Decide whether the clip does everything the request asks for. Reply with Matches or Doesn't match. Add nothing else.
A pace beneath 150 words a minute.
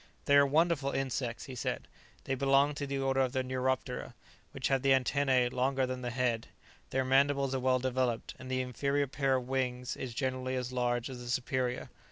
Doesn't match